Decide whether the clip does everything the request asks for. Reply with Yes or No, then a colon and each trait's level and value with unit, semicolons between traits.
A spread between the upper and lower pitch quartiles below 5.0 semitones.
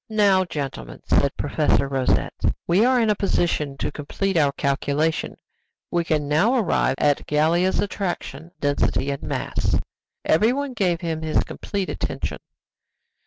No: wide, 5.4 semitones